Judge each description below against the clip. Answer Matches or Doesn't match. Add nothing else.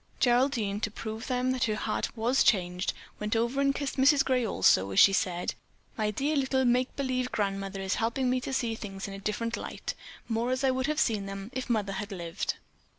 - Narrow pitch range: Doesn't match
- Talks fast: Matches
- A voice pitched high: Matches